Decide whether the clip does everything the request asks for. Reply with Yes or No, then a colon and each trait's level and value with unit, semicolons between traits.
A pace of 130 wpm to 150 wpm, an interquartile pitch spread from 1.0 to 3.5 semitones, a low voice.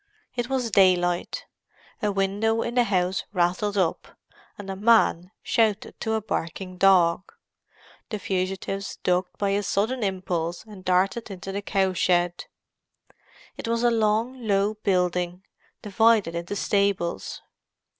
No: slow, 135 wpm; average, 3.1 semitones; high, 195 Hz